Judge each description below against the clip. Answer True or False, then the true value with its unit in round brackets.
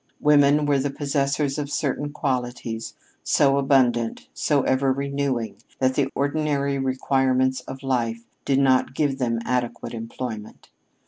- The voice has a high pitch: False (135 Hz)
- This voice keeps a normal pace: False (130 wpm)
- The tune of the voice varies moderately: False (1.9 semitones)